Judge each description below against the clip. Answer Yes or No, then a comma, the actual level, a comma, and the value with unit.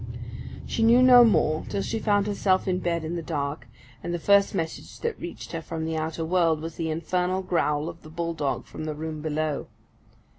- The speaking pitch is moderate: Yes, medium, 165 Hz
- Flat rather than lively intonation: No, average, 3.0 semitones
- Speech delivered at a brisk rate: Yes, fast, 210 wpm